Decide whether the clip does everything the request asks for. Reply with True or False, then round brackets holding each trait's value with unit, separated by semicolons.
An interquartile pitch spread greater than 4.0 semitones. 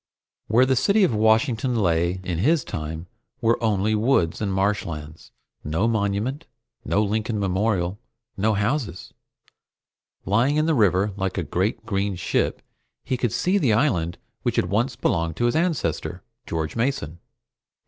True (4.8 semitones)